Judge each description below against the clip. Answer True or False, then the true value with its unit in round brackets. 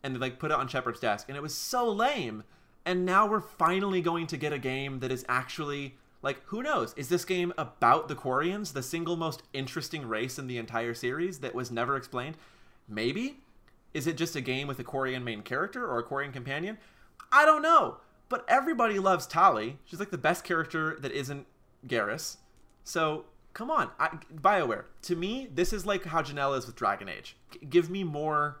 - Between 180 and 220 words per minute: True (205 wpm)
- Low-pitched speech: False (150 Hz)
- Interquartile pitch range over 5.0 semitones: True (5.5 semitones)